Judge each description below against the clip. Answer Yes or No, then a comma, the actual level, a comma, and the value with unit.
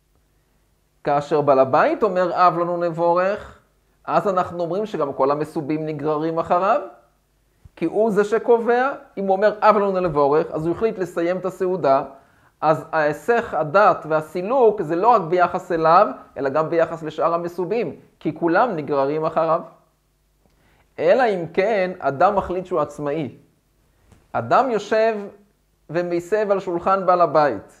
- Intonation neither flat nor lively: Yes, average, 3.8 semitones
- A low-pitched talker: No, medium, 175 Hz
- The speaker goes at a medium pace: Yes, average, 135 wpm